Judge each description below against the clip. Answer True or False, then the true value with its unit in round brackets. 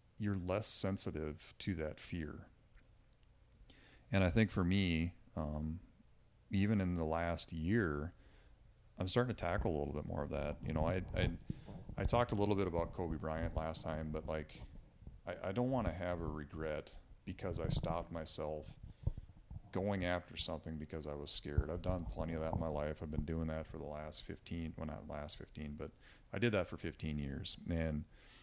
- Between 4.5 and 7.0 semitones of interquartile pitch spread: False (3.8 semitones)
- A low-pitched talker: True (85 Hz)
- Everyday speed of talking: True (190 wpm)